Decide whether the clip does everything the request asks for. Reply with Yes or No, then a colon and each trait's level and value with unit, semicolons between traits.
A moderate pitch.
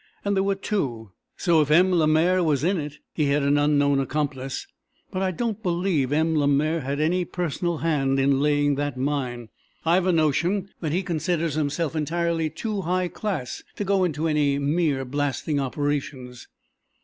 Yes: medium, 155 Hz